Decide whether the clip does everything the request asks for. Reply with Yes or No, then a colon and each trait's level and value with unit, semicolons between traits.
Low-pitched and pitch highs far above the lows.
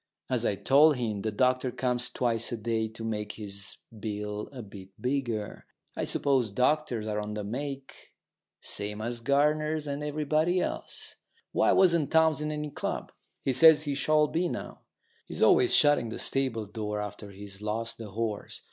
Yes: low, 120 Hz; wide, 5.7 semitones